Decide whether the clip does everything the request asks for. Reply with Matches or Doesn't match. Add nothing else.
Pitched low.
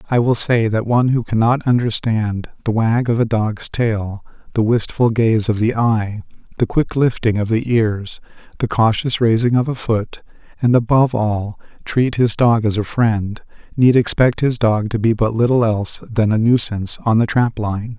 Matches